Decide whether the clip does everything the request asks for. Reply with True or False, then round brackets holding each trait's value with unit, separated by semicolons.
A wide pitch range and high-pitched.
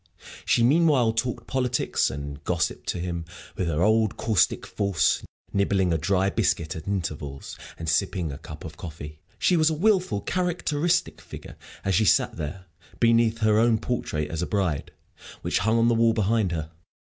False (6.1 semitones; 100 Hz)